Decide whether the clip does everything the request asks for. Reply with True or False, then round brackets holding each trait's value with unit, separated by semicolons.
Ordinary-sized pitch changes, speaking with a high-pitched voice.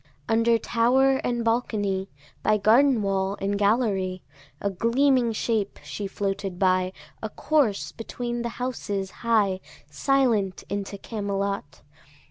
True (3.3 semitones; 215 Hz)